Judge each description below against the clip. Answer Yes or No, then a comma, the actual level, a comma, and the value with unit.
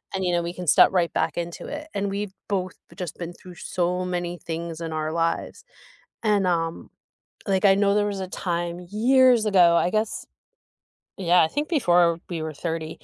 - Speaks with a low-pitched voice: No, medium, 180 Hz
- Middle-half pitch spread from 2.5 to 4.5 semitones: Yes, average, 2.9 semitones